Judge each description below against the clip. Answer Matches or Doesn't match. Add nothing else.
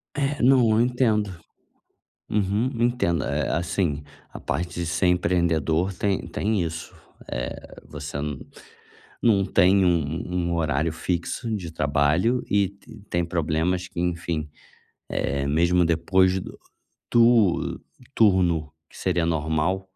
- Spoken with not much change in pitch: Doesn't match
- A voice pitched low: Matches